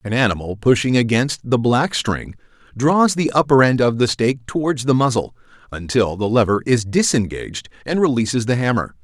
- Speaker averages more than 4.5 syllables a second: Yes, 5.3 syllables/s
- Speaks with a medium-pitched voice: No, low, 125 Hz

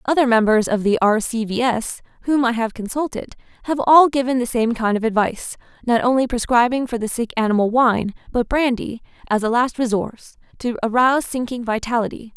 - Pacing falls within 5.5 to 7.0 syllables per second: Yes, 5.6 syllables/s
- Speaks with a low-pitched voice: No, high, 240 Hz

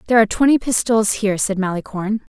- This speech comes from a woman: Yes, female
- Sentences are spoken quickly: No, average, 180 wpm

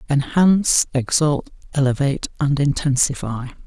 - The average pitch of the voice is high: No, medium, 140 Hz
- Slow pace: Yes, slow, 80 wpm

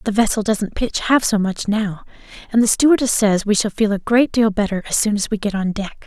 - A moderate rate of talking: No, fast, 255 wpm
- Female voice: Yes, female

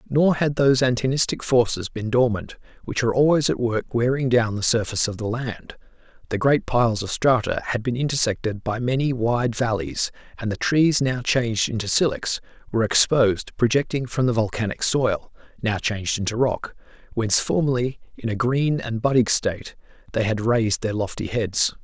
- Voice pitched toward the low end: Yes, low, 120 Hz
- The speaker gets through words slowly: No, average, 175 wpm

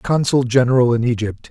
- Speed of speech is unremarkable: Yes, average, 160 wpm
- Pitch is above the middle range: No, low, 125 Hz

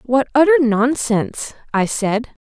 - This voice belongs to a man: No, female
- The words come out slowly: Yes, slow, 120 wpm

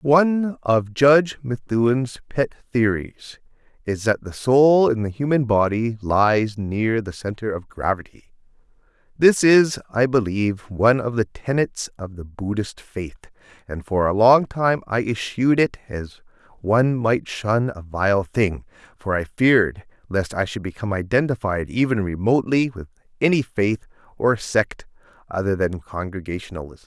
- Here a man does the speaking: Yes, male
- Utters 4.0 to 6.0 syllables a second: Yes, 4.5 syllables/s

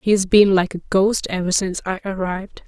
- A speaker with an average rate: No, fast, 225 wpm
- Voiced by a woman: Yes, female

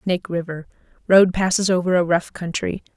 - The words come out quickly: No, average, 140 wpm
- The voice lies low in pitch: No, medium, 180 Hz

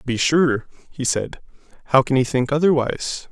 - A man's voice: Yes, male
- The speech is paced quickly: No, average, 180 wpm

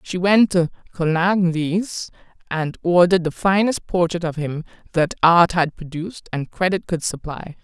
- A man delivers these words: No, female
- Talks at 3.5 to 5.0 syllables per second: Yes, 4.5 syllables/s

